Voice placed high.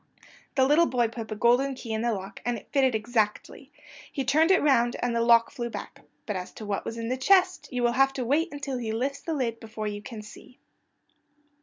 Yes: high, 240 Hz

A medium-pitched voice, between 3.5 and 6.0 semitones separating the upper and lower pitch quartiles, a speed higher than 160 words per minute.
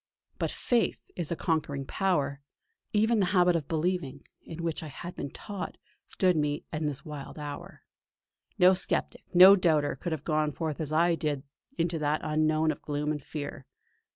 No: medium, 155 Hz; average, 3.1 semitones; average, 180 wpm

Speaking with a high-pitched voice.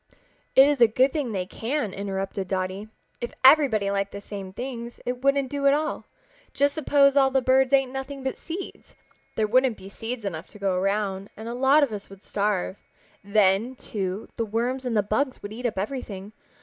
Yes: high, 230 Hz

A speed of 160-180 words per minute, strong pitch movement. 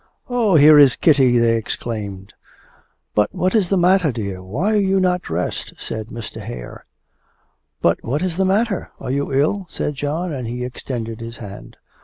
Yes: average, 175 wpm; wide, 8.1 semitones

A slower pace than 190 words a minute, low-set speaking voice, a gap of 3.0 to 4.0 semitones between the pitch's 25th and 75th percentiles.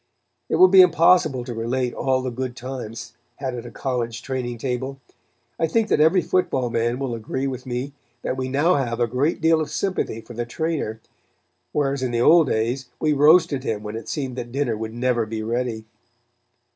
No: average, 195 wpm; low, 130 Hz; average, 3.5 semitones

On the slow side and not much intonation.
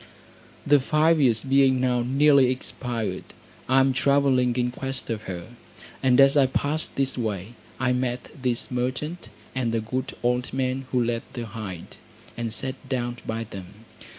No: average, 160 wpm; narrow, 2.3 semitones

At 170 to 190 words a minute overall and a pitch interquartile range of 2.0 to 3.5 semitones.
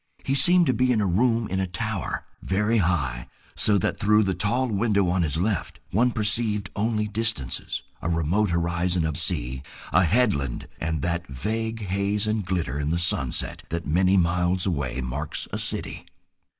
No: average, 175 wpm; average, 4.4 semitones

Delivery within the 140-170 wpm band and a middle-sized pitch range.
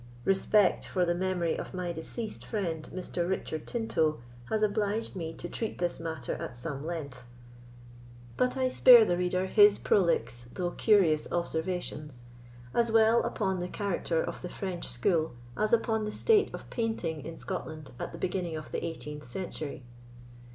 Yes: average, 160 wpm; average, 4.6 semitones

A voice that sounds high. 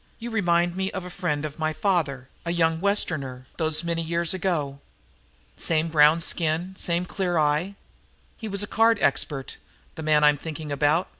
No: medium, 165 Hz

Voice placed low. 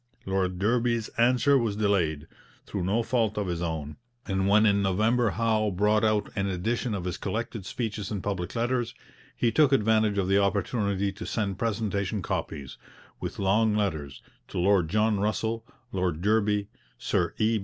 Yes: low, 105 Hz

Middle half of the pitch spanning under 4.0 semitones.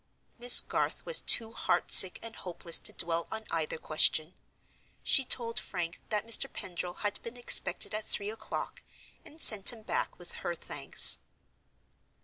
No: average, 4.8 semitones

